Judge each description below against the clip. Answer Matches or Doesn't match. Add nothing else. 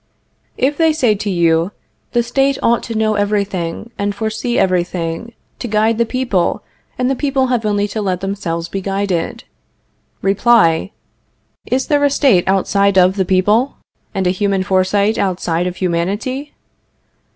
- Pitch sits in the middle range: Doesn't match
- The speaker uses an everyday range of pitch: Matches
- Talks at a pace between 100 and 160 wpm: Matches